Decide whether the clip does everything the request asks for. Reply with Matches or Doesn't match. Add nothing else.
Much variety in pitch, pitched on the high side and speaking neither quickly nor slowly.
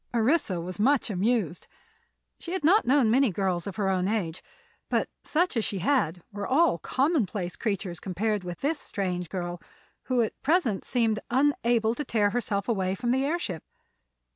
Matches